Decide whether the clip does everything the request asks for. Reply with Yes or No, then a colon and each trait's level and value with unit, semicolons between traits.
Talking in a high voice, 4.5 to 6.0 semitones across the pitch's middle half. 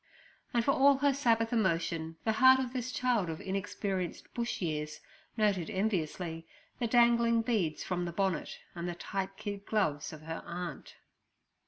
Yes: high, 195 Hz; wide, 5.6 semitones